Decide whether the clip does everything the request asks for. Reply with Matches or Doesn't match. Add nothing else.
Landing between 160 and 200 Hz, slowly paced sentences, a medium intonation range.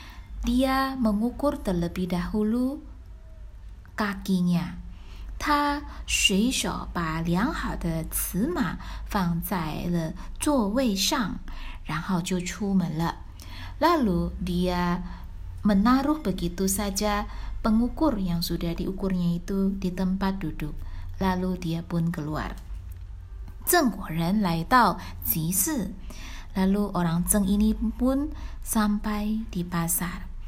Matches